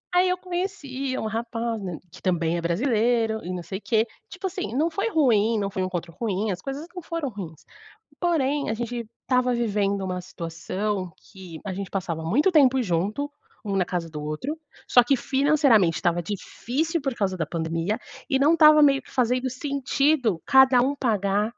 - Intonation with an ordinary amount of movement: No, wide, 6.6 semitones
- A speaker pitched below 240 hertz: Yes, high, 230 Hz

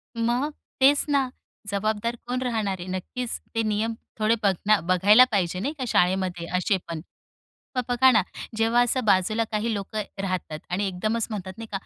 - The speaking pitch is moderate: No, high, 215 Hz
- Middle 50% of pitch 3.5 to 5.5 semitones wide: Yes, average, 3.9 semitones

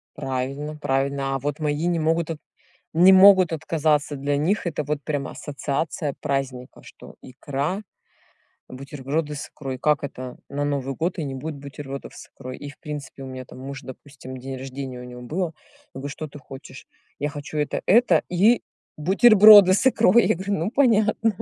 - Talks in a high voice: No, medium, 145 Hz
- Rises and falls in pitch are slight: No, average, 3.6 semitones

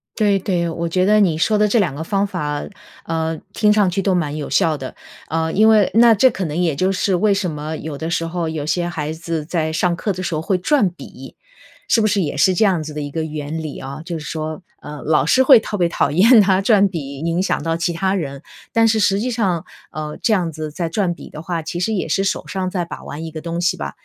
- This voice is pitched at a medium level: Yes, medium, 170 Hz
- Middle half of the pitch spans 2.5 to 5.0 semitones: Yes, average, 3.8 semitones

